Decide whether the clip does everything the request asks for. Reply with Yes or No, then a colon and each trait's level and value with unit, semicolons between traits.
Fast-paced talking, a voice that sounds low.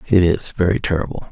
No: average, 180 wpm; very low, 90 Hz